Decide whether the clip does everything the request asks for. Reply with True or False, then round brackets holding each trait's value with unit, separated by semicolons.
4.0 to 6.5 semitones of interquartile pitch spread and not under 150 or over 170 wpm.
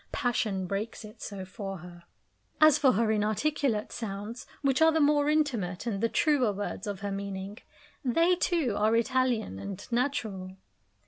True (5.2 semitones; 155 wpm)